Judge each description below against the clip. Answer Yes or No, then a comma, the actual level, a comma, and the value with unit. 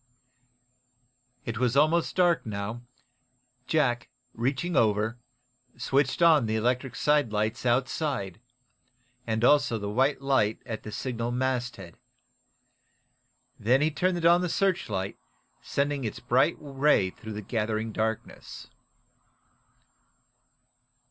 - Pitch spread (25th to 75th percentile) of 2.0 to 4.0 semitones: No, average, 4.7 semitones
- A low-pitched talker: Yes, low, 125 Hz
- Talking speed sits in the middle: No, slow, 105 wpm